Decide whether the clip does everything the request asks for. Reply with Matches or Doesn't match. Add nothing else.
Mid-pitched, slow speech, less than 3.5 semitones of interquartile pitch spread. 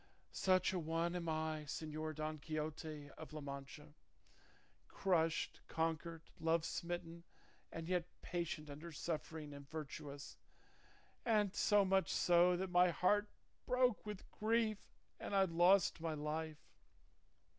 Matches